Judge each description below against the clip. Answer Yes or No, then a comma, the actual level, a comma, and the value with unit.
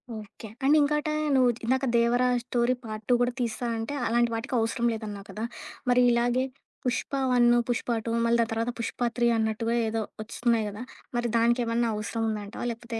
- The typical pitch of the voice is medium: No, high, 235 Hz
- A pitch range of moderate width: No, narrow, 1.4 semitones